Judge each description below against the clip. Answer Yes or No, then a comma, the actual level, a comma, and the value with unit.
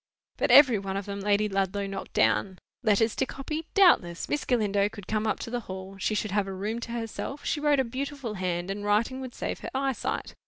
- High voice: Yes, high, 215 Hz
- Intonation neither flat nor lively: Yes, average, 4.8 semitones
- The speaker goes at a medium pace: No, fast, 225 wpm